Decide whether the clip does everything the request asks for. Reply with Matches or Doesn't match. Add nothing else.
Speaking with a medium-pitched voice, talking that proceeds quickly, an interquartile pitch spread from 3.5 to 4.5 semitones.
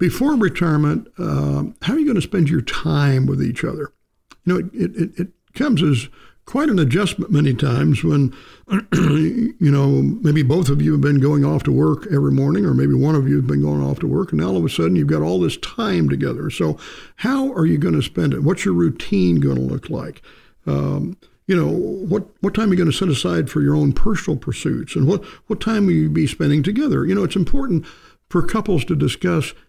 Doesn't match